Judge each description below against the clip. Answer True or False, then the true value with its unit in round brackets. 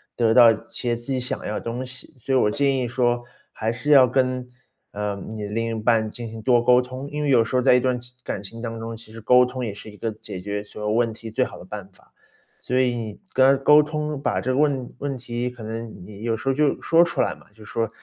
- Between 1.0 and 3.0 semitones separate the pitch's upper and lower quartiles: True (2.5 semitones)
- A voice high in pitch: False (120 Hz)